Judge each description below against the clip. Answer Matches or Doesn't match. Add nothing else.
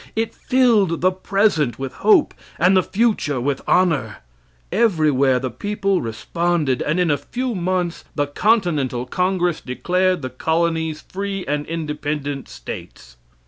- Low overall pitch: Doesn't match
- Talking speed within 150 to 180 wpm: Doesn't match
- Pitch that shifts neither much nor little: Matches